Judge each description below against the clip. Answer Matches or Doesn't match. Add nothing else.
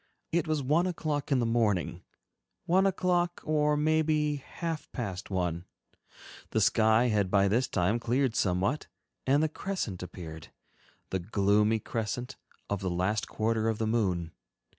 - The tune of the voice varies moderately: Doesn't match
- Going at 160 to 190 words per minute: Doesn't match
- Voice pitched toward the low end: Matches